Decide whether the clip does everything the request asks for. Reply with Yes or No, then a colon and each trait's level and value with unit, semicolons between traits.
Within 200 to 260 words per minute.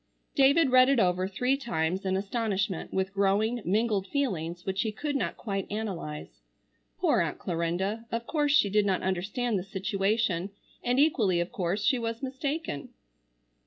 No: average, 160 wpm